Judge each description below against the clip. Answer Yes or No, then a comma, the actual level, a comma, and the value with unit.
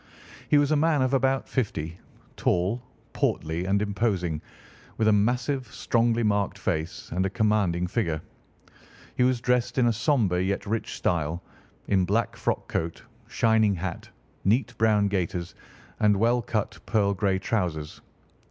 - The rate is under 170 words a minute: Yes, average, 145 wpm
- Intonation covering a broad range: No, average, 4.7 semitones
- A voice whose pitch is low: Yes, low, 105 Hz